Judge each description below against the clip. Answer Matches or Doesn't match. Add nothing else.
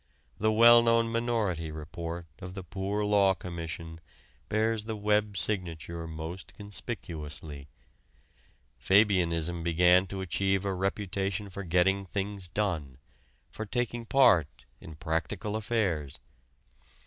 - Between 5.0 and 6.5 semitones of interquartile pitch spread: Doesn't match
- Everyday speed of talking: Doesn't match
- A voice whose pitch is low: Matches